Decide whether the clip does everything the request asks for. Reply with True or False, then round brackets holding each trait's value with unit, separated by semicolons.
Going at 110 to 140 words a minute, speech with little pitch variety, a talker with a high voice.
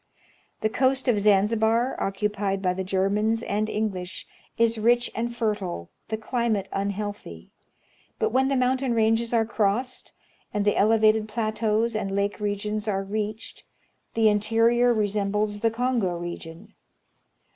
True (135 wpm; 2.2 semitones; 215 Hz)